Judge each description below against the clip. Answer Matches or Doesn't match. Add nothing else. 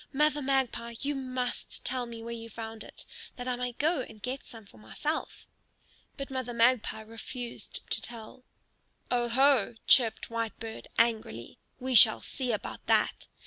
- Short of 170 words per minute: Matches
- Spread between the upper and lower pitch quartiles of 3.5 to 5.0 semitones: Doesn't match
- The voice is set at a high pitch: Matches